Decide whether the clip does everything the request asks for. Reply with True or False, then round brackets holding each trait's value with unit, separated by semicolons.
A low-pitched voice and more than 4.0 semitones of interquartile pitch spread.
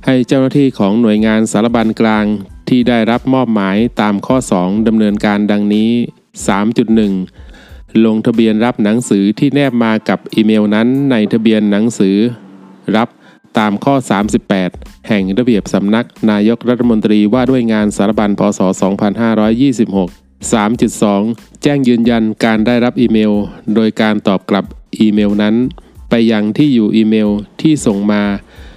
False (110 Hz; 2.5 semitones)